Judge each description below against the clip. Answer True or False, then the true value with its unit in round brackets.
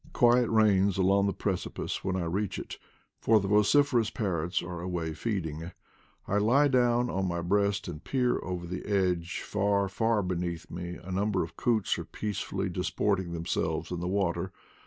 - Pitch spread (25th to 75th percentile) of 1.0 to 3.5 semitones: True (3.1 semitones)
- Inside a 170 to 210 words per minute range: True (175 wpm)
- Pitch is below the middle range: True (95 Hz)